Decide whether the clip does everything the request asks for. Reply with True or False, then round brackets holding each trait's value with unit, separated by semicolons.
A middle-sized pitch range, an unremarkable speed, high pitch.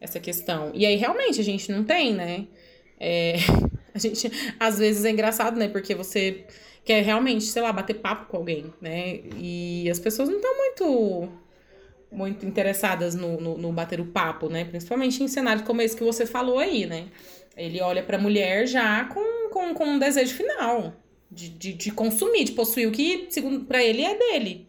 False (4.9 semitones; 190 wpm; 215 Hz)